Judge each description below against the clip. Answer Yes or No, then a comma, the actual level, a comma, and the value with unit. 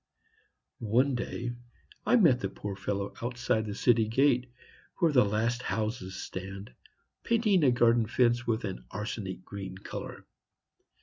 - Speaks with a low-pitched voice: Yes, low, 115 Hz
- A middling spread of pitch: Yes, average, 3.6 semitones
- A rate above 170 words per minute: No, slow, 135 wpm